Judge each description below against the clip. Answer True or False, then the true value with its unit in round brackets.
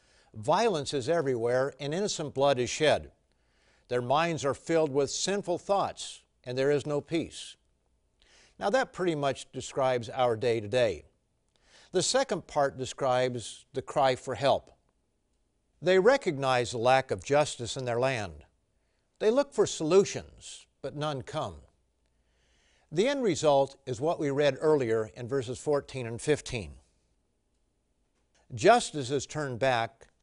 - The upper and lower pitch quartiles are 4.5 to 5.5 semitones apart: True (5.2 semitones)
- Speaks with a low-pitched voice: True (130 Hz)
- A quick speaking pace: False (140 wpm)